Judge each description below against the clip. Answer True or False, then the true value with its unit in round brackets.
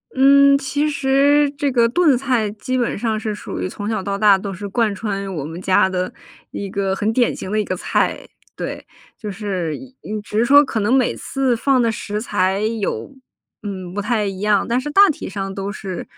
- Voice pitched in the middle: False (215 Hz)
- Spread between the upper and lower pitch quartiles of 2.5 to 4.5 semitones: False (4.9 semitones)